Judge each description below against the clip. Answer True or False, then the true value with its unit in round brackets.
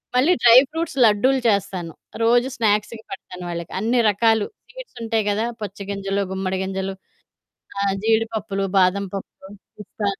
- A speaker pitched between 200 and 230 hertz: True (210 Hz)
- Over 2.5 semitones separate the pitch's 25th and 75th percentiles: True (2.9 semitones)